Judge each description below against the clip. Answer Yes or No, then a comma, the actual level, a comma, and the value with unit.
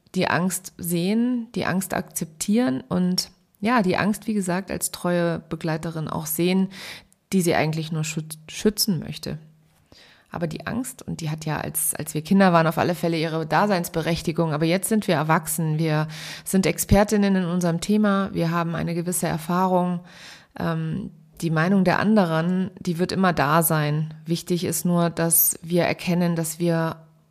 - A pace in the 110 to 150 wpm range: No, average, 165 wpm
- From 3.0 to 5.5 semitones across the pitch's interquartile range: No, narrow, 2.4 semitones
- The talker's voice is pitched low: No, medium, 175 Hz